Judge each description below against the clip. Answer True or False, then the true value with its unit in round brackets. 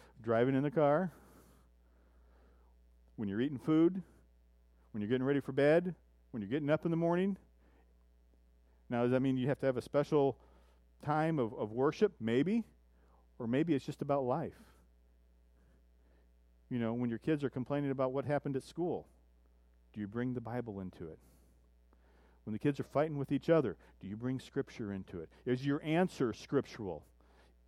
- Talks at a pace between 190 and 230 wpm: False (170 wpm)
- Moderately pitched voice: False (110 Hz)